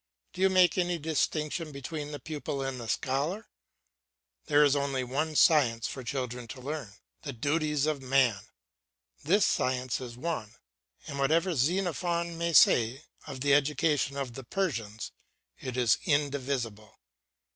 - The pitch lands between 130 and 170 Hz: Yes, medium, 140 Hz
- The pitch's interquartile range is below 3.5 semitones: No, average, 3.9 semitones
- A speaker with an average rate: Yes, average, 145 wpm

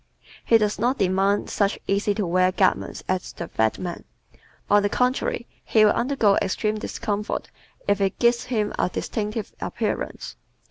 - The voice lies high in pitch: Yes, high, 205 Hz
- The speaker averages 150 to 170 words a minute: Yes, average, 155 wpm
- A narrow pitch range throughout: Yes, narrow, 2.2 semitones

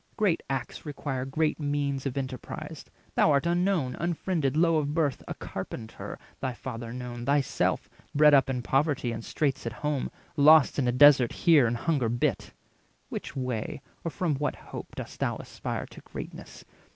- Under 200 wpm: Yes, average, 165 wpm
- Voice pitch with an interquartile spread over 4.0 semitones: No, average, 3.3 semitones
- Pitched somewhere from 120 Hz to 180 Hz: Yes, medium, 140 Hz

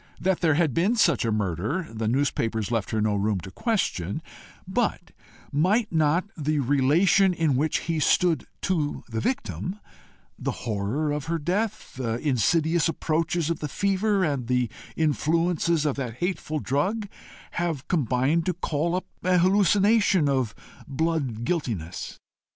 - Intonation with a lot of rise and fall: Yes, wide, 5.9 semitones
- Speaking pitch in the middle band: Yes, medium, 155 Hz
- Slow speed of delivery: No, average, 145 wpm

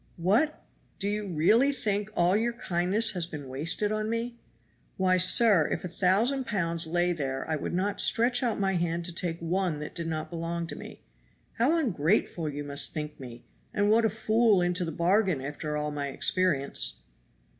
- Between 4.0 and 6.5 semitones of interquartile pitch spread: Yes, average, 4.8 semitones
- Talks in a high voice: No, medium, 180 Hz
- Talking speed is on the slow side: No, average, 185 wpm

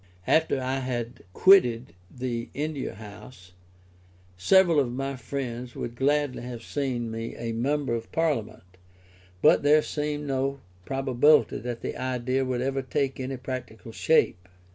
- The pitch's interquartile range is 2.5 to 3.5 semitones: Yes, average, 2.9 semitones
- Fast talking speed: No, average, 140 wpm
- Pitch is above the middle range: No, low, 130 Hz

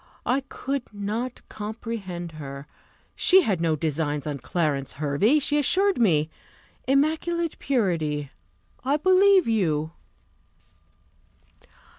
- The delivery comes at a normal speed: No, slow, 100 wpm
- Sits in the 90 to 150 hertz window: No, high, 205 Hz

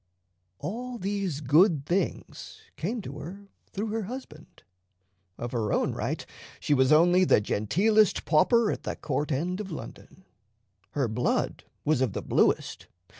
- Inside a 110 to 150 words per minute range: Yes, average, 145 wpm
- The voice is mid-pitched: Yes, medium, 170 Hz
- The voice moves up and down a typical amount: No, wide, 6.3 semitones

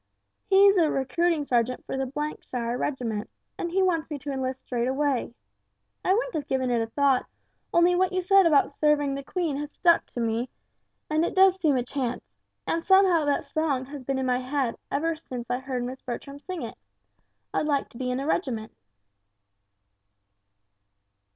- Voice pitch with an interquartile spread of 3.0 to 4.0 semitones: No, average, 4.7 semitones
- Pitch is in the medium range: No, very high, 280 Hz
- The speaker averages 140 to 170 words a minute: No, average, 185 wpm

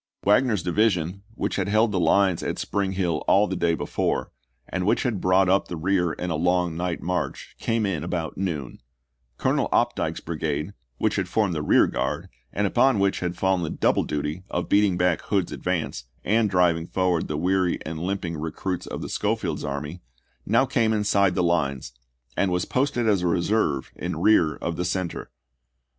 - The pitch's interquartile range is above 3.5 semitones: No, average, 3.1 semitones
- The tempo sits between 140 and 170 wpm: No, average, 185 wpm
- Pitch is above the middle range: No, very low, 90 Hz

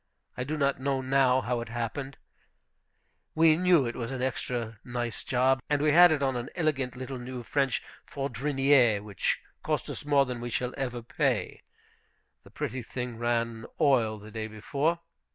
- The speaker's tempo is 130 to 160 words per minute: No, average, 175 wpm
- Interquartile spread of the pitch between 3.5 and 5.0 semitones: No, average, 2.8 semitones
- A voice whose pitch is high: No, low, 130 Hz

